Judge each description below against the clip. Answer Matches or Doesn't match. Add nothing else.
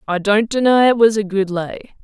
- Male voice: Doesn't match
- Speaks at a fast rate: Matches